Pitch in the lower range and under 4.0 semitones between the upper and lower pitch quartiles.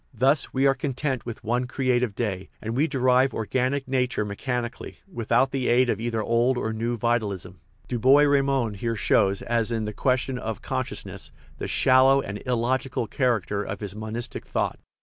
Yes: low, 120 Hz; average, 2.9 semitones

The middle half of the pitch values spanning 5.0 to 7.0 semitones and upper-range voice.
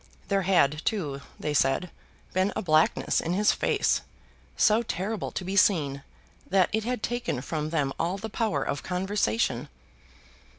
No: wide, 5.5 semitones; medium, 180 Hz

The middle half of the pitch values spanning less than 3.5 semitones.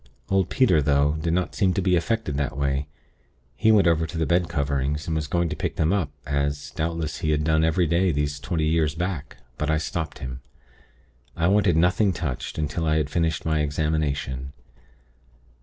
Yes: average, 2.9 semitones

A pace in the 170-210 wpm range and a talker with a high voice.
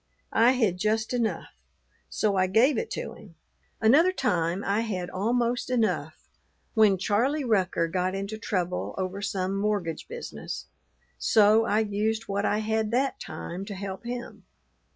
No: average, 150 wpm; high, 210 Hz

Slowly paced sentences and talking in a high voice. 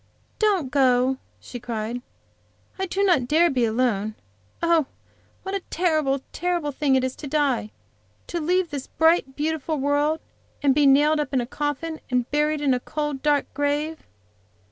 No: average, 165 wpm; very high, 290 Hz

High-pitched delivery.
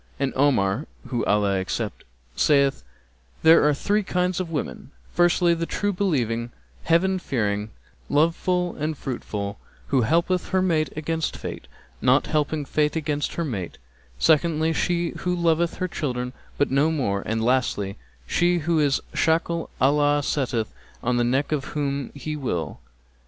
No: medium, 150 Hz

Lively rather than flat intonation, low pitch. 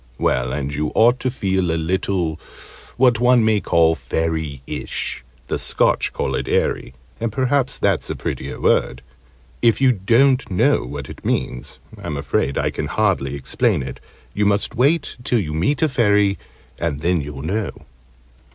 Yes: wide, 8.2 semitones; very low, 90 Hz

